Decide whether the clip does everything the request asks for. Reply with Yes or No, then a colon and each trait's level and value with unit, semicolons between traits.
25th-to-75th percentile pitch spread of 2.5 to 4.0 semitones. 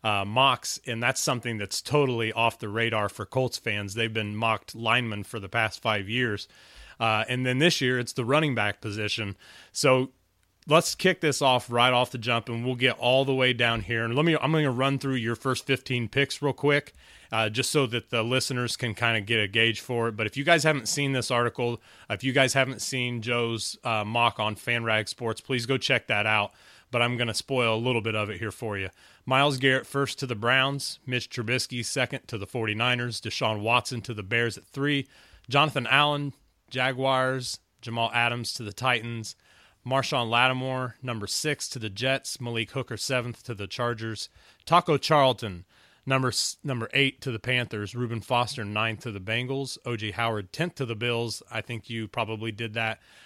Yes: average, 2.8 semitones